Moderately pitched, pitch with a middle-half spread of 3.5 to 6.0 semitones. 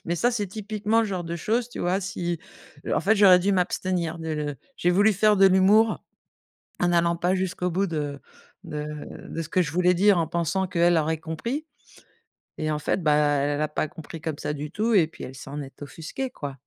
Yes: medium, 175 Hz; average, 4.1 semitones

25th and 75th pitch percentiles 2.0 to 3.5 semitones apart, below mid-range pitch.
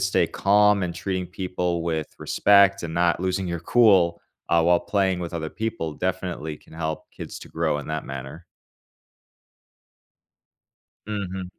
Yes: average, 2.7 semitones; very low, 90 Hz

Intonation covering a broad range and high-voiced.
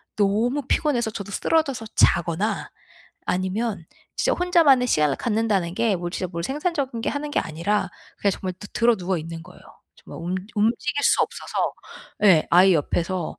Yes: wide, 5.7 semitones; high, 205 Hz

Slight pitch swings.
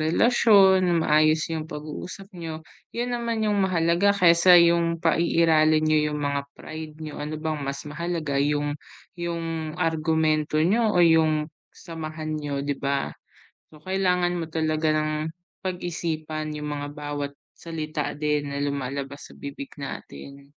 Yes: narrow, 2.3 semitones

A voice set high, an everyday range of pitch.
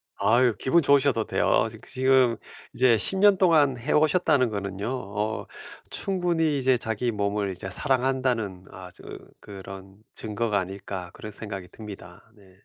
No: low, 115 Hz; average, 4.9 semitones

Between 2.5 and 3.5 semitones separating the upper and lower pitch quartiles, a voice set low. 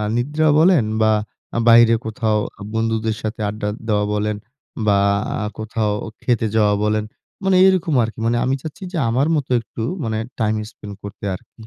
Yes: average, 3.0 semitones; low, 110 Hz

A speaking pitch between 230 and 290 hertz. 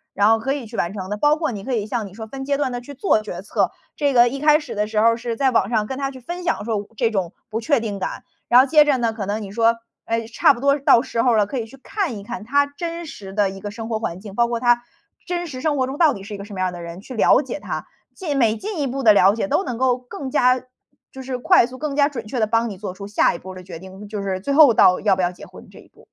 Yes: high, 235 Hz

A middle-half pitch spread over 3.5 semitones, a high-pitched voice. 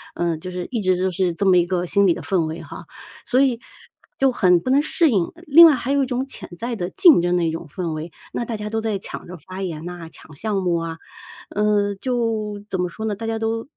Yes: average, 4.5 semitones; high, 195 Hz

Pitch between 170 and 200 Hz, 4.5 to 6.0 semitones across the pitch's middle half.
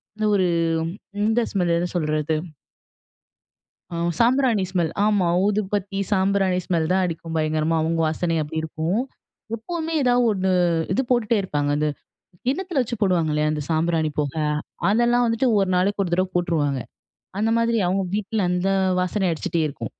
Yes: medium, 185 Hz; average, 4.9 semitones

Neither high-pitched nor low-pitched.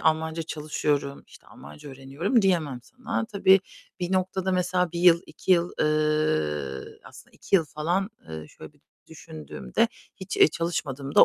Yes: medium, 160 Hz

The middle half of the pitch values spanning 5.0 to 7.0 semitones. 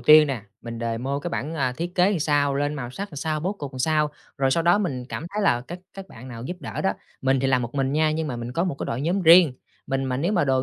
No: average, 4.4 semitones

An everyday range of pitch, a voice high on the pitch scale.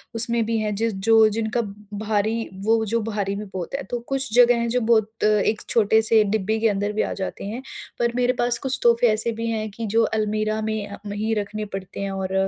No: narrow, 1.8 semitones; high, 220 Hz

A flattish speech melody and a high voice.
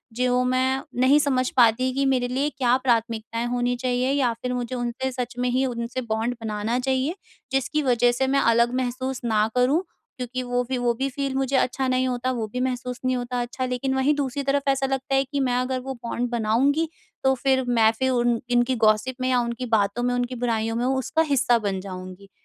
Yes: narrow, 1.7 semitones; very high, 250 Hz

